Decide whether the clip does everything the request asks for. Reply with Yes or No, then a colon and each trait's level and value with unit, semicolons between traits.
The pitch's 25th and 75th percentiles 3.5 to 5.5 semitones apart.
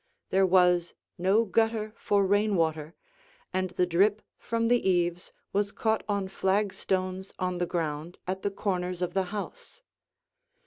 No: narrow, 2.5 semitones